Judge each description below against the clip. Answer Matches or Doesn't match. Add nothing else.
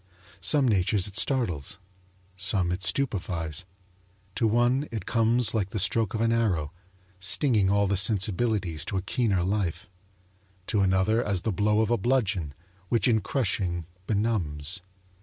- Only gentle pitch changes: Doesn't match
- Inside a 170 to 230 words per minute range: Doesn't match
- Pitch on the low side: Matches